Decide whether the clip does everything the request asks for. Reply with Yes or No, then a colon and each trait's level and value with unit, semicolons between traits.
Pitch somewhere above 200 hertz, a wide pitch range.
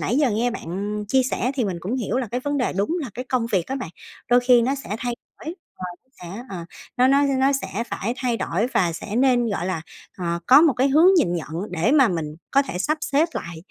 Yes: high, 240 Hz; wide, 5.7 semitones